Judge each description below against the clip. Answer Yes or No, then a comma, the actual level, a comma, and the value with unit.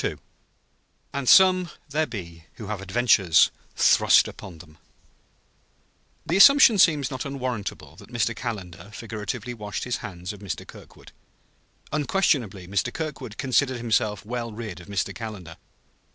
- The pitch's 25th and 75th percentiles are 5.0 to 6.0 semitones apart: Yes, wide, 5.4 semitones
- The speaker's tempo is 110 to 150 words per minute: Yes, slow, 135 wpm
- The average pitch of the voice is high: No, low, 115 Hz